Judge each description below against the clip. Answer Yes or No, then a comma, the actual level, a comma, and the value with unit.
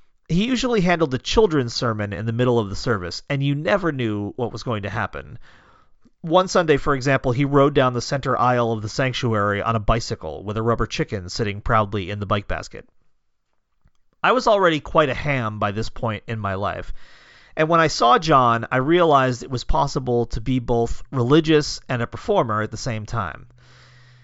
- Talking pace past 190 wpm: Yes, average, 200 wpm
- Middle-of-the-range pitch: No, low, 120 Hz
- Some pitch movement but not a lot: Yes, average, 4.5 semitones